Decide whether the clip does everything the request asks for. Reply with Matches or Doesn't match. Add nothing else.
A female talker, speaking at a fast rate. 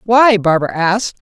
Doesn't match